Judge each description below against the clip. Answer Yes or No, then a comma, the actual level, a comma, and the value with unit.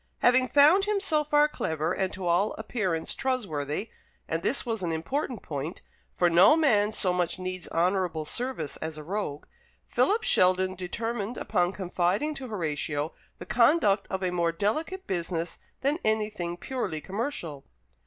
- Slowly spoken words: No, average, 155 wpm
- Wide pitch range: Yes, wide, 6.4 semitones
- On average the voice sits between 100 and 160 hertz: No, high, 190 Hz